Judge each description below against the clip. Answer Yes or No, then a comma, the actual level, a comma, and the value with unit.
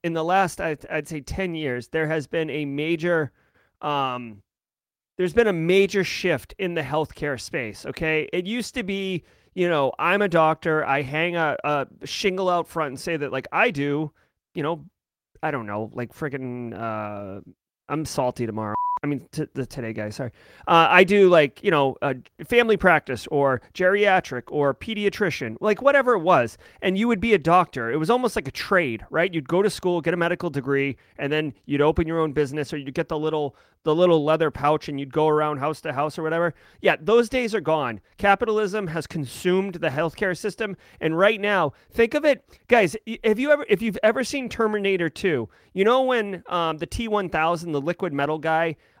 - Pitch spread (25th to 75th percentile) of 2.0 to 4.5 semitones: No, average, 5.1 semitones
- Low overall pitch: No, medium, 160 Hz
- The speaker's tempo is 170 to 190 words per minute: No, average, 200 wpm